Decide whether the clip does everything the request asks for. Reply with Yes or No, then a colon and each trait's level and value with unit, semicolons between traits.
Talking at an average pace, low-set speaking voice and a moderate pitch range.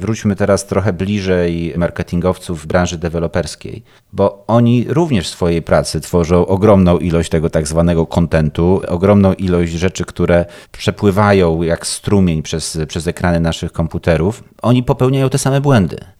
Yes: average, 140 wpm; very low, 90 Hz; average, 3.2 semitones